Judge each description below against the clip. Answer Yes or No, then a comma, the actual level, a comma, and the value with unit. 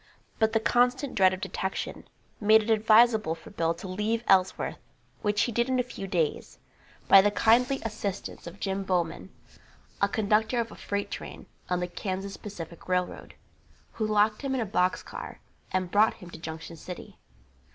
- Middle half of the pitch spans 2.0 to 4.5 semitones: Yes, average, 3.3 semitones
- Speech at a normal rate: Yes, average, 175 wpm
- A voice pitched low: No, high, 205 Hz